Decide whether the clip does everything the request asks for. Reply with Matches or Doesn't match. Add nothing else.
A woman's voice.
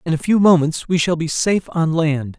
Doesn't match